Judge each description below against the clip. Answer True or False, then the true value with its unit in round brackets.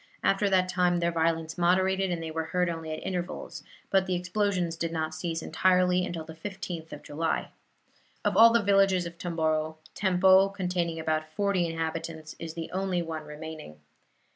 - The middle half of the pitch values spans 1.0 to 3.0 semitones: True (2.6 semitones)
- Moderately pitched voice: True (170 Hz)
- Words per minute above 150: True (170 wpm)